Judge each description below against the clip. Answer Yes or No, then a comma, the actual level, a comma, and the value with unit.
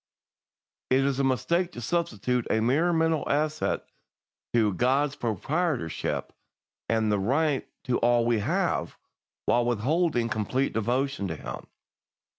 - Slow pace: Yes, slow, 120 wpm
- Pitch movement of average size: Yes, average, 4.7 semitones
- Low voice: Yes, low, 130 Hz